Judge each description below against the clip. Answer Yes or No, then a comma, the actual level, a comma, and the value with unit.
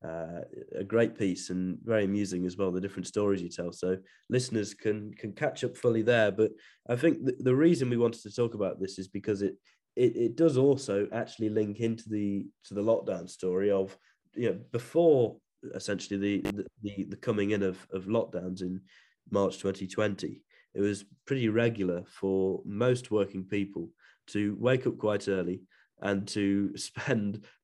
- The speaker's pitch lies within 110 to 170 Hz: No, low, 100 Hz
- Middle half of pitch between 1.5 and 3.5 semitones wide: Yes, average, 3.2 semitones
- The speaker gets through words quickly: No, average, 180 wpm